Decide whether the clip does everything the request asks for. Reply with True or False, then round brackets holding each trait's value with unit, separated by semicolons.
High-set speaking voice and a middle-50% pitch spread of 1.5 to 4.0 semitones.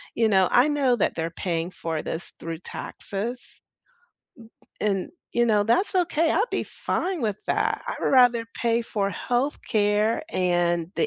False (215 Hz; 5.3 semitones)